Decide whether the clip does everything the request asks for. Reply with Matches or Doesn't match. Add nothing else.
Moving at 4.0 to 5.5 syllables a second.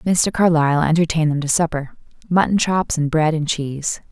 Matches